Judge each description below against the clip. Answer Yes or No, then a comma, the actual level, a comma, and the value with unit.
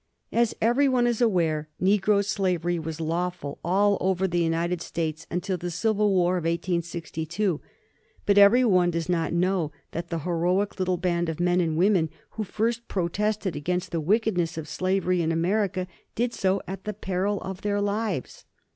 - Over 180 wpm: No, average, 170 wpm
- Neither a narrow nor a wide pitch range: Yes, average, 3.2 semitones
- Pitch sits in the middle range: Yes, medium, 180 Hz